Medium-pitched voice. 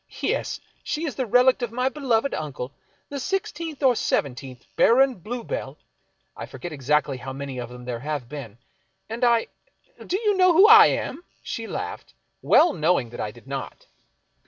No: high, 225 Hz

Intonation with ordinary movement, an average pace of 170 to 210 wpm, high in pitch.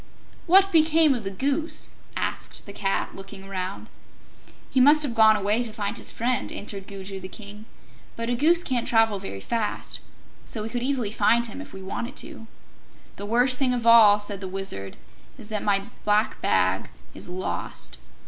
Yes: average, 4.2 semitones; average, 180 wpm; high, 220 Hz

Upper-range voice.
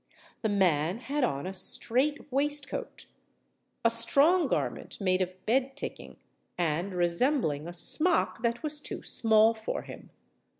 Yes: high, 225 Hz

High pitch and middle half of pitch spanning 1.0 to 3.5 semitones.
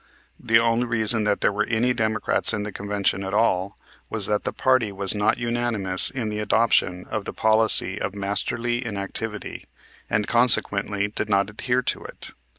No: low, 105 Hz; narrow, 2.4 semitones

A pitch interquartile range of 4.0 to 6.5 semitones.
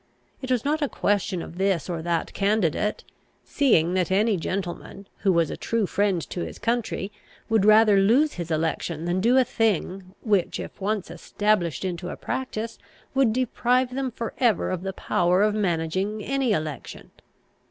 Yes: average, 4.4 semitones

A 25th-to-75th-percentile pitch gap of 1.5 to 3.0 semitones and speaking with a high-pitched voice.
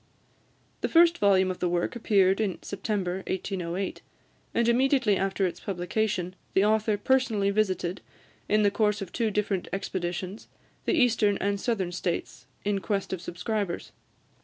Yes: average, 2.7 semitones; high, 200 Hz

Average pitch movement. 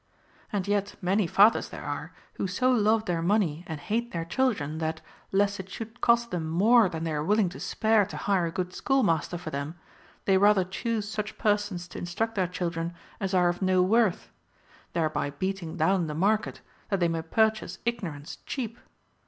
Yes: average, 4.2 semitones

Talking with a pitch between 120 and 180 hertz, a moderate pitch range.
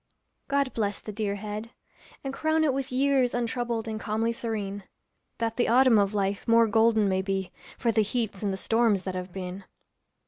No: high, 220 Hz; average, 3.1 semitones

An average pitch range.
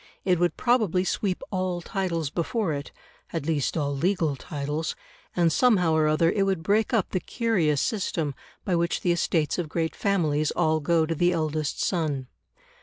Yes: average, 3.3 semitones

